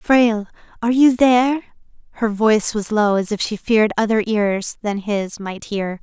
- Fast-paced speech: No, average, 180 wpm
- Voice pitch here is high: Yes, high, 215 Hz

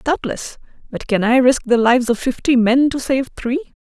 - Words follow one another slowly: No, fast, 205 wpm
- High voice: Yes, very high, 255 Hz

